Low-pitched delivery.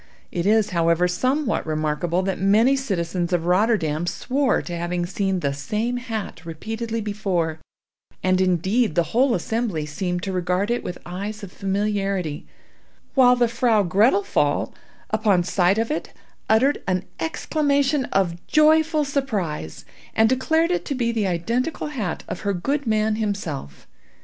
No: high, 200 Hz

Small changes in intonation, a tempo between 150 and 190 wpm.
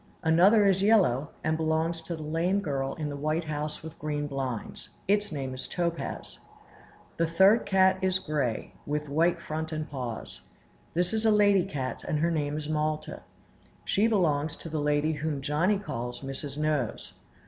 No: average, 3.3 semitones; average, 170 wpm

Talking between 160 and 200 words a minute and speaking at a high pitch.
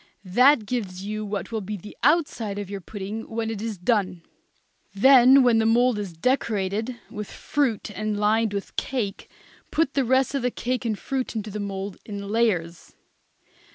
Yes: average, 175 wpm; high, 215 Hz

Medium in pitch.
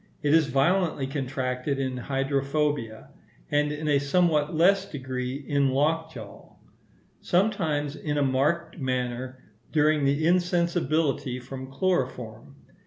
Yes: medium, 145 Hz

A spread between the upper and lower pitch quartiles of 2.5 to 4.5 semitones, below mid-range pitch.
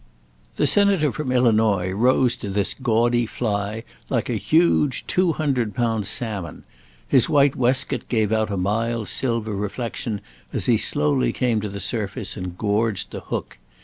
Yes: average, 3.8 semitones; low, 115 Hz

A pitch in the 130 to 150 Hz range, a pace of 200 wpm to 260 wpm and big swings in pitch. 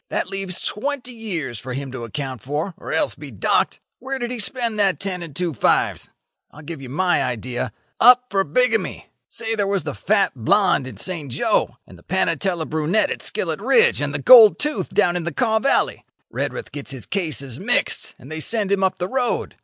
No: medium, 185 Hz; fast, 205 wpm; wide, 7.5 semitones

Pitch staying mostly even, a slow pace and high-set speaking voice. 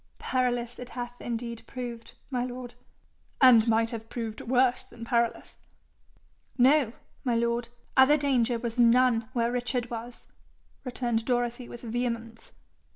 Yes: narrow, 1.3 semitones; slow, 130 wpm; high, 240 Hz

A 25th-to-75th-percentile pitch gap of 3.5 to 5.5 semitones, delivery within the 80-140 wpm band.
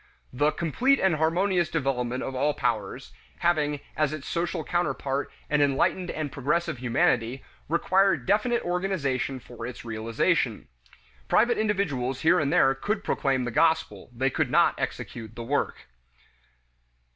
Yes: average, 5.2 semitones; slow, 135 wpm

